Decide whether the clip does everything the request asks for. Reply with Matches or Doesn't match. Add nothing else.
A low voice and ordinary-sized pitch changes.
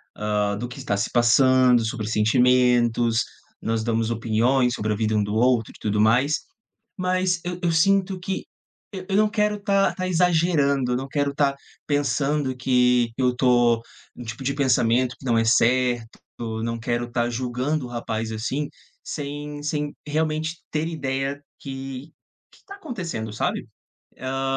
Matches